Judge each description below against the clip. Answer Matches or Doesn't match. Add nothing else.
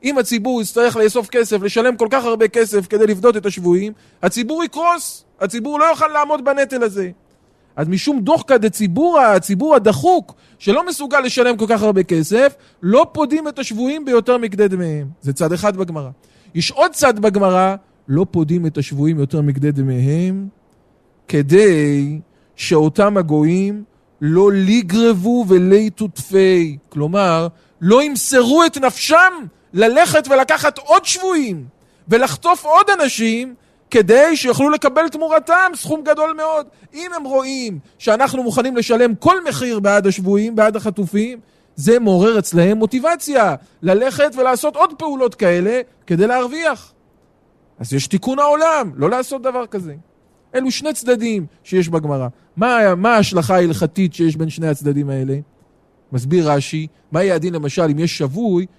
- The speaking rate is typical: Matches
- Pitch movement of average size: Doesn't match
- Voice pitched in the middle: Doesn't match